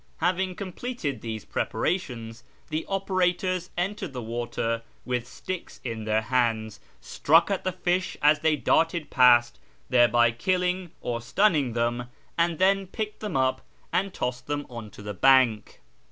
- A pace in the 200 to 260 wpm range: No, average, 145 wpm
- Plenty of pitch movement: Yes, wide, 7.4 semitones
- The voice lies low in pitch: No, medium, 145 Hz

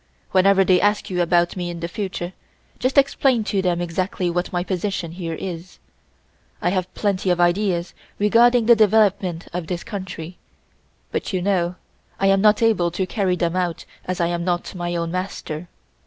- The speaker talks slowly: No, average, 180 wpm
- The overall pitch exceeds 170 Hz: Yes, medium, 185 Hz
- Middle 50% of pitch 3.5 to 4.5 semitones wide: No, narrow, 2.4 semitones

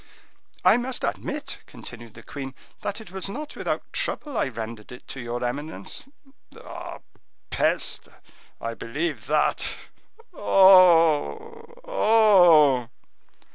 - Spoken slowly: Yes, slow, 110 wpm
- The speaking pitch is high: No, medium, 160 Hz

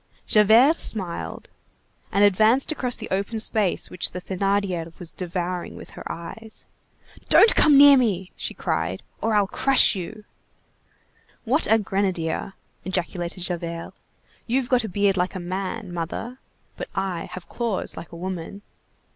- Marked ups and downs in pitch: No, average, 3.9 semitones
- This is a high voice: Yes, high, 195 Hz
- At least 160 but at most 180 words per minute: No, average, 145 wpm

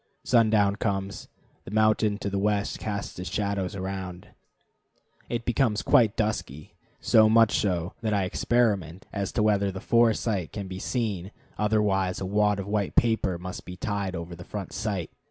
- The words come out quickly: No, average, 170 wpm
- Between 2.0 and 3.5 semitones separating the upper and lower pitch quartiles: Yes, narrow, 2.4 semitones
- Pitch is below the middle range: Yes, low, 100 Hz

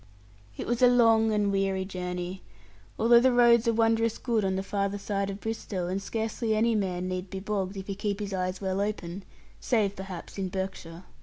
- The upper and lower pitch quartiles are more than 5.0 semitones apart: No, average, 2.8 semitones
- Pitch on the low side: No, high, 200 Hz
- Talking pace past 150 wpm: Yes, average, 200 wpm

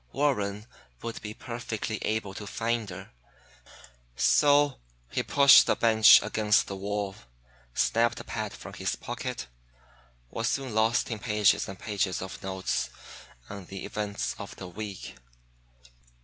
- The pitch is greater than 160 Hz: No, low, 105 Hz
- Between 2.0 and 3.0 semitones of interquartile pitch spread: Yes, narrow, 2.6 semitones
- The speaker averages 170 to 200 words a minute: No, slow, 135 wpm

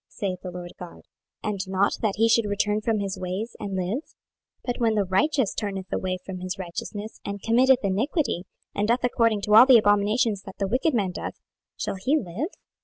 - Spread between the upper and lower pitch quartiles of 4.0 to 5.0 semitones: No, average, 3.4 semitones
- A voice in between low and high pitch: No, high, 205 Hz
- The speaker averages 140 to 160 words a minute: No, average, 200 wpm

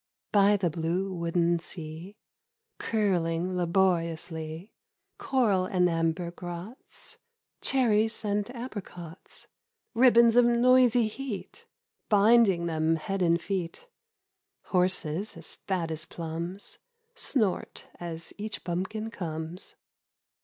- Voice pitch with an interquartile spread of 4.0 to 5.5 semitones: Yes, average, 4.6 semitones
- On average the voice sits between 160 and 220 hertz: Yes, medium, 185 Hz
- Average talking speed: No, slow, 100 wpm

